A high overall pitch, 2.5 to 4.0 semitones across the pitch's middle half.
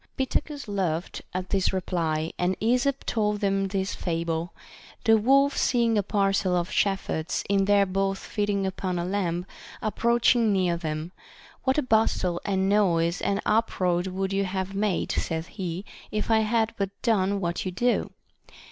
Yes: high, 195 Hz; average, 3.1 semitones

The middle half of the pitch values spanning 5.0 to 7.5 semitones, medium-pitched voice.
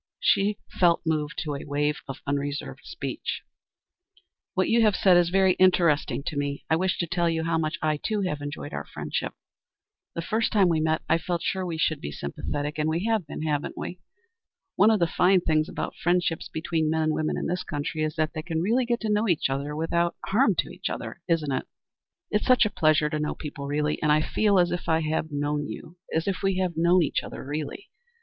No: average, 3.3 semitones; medium, 165 Hz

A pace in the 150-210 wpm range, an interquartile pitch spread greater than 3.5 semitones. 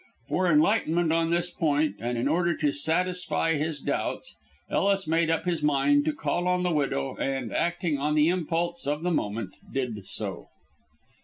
No: average, 170 wpm; average, 3.2 semitones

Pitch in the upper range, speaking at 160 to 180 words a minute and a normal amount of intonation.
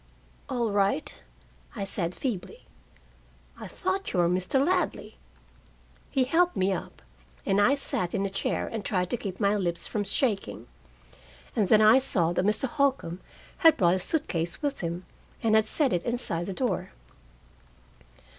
No: high, 205 Hz; average, 165 wpm; wide, 6.4 semitones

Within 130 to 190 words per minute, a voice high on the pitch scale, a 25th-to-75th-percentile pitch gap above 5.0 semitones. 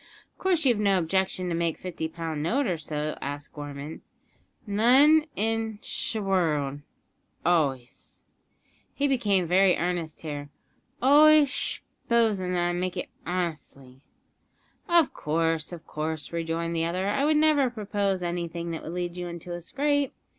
No: average, 150 wpm; medium, 175 Hz; wide, 5.5 semitones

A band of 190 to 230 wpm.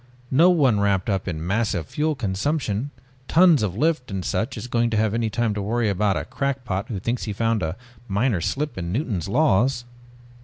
Yes: average, 195 wpm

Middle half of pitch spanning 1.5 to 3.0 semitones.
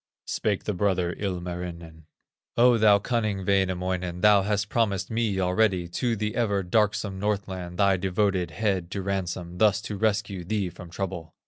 Yes: average, 2.7 semitones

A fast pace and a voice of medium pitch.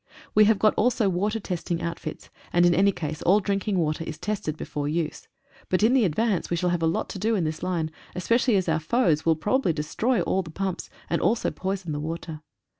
Yes: fast, 220 wpm; medium, 180 Hz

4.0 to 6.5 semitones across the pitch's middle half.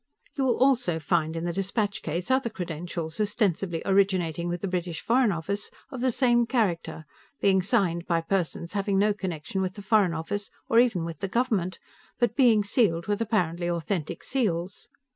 Yes: average, 4.3 semitones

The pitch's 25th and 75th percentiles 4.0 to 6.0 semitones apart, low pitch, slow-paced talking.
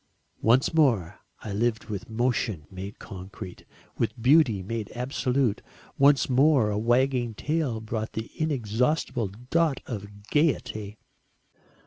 Yes: average, 4.3 semitones; low, 120 Hz; slow, 115 wpm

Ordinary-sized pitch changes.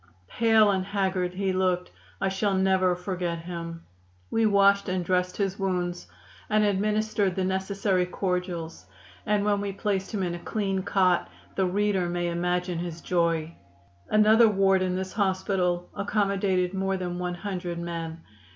No: narrow, 2.0 semitones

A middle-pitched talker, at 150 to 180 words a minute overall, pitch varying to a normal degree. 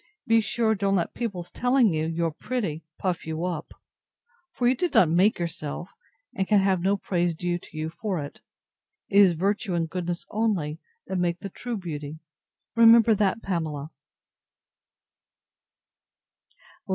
Yes: medium, 180 Hz; average, 155 wpm; average, 4.2 semitones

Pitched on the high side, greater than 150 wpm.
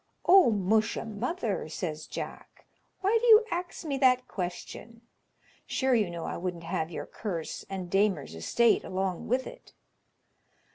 No: high, 210 Hz; average, 145 wpm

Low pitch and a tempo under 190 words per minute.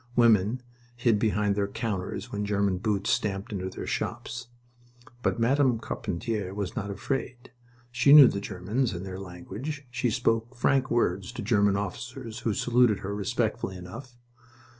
Yes: low, 110 Hz; average, 150 wpm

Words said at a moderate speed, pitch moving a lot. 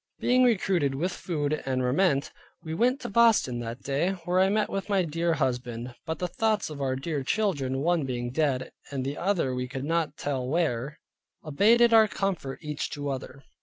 Yes: average, 190 wpm; wide, 6.0 semitones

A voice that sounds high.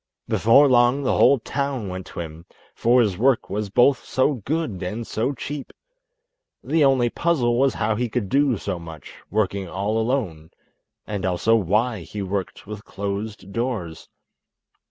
No: low, 110 Hz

